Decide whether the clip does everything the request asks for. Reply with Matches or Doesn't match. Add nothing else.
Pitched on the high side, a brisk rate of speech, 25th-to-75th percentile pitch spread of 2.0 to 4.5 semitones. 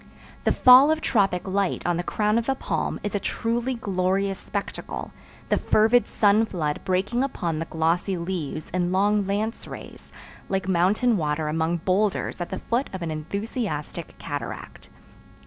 Doesn't match